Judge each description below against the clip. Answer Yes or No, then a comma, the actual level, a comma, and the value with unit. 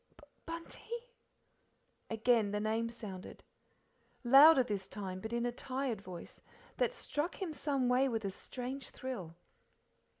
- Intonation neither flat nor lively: Yes, average, 4.6 semitones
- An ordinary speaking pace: No, slow, 130 wpm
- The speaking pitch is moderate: No, high, 240 Hz